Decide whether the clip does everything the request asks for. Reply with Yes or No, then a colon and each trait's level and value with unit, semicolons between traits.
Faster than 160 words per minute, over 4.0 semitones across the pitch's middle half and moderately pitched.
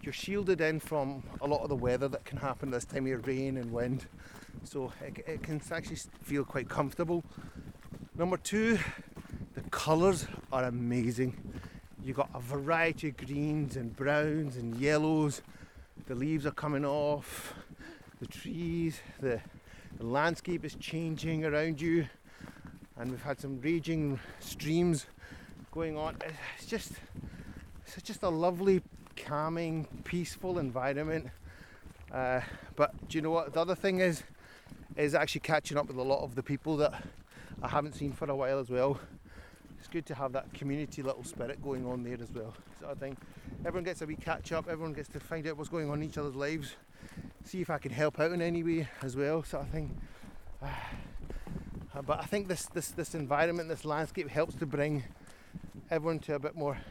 No: average, 180 wpm; average, 3.3 semitones; medium, 150 Hz